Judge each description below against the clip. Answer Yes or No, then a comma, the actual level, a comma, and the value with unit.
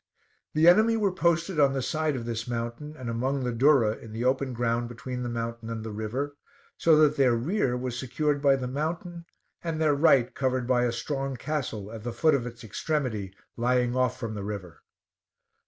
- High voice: No, low, 125 Hz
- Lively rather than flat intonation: No, average, 4.3 semitones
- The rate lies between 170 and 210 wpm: Yes, average, 200 wpm